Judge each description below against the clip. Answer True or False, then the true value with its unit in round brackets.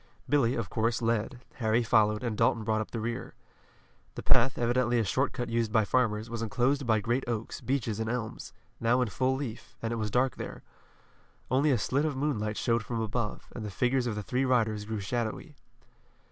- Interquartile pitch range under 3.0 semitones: True (2.4 semitones)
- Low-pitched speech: True (115 Hz)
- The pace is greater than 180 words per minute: True (200 wpm)